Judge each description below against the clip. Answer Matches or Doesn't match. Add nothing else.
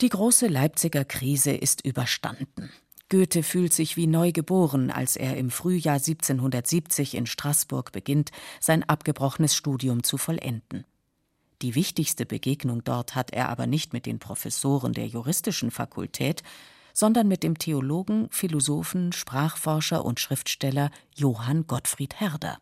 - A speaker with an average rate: Matches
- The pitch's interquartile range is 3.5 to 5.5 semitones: Matches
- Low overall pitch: Doesn't match